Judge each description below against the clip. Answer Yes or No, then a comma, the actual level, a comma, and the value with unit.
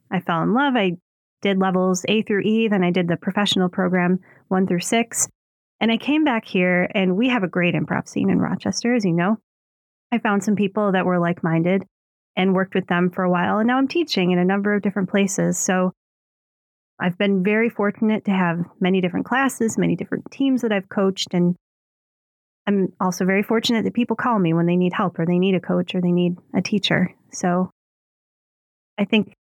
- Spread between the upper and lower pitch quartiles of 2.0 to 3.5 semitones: Yes, average, 3.0 semitones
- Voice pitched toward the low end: No, high, 190 Hz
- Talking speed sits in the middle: No, fast, 210 wpm